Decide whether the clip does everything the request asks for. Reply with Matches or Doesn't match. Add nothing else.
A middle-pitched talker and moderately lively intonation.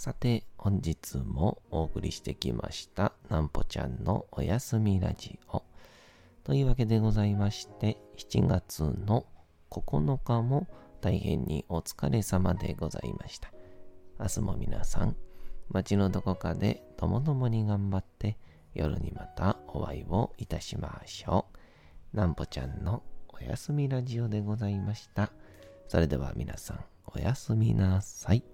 Doesn't match